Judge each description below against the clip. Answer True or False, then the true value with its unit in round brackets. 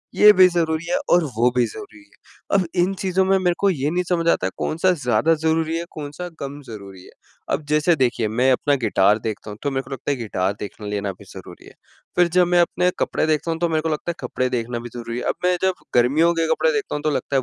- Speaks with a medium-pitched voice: True (150 Hz)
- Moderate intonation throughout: False (6.4 semitones)